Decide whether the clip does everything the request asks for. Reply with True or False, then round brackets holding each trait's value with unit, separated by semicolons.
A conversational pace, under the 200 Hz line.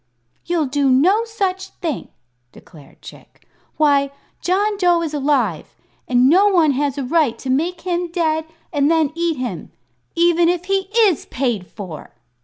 False (155 wpm; 320 Hz)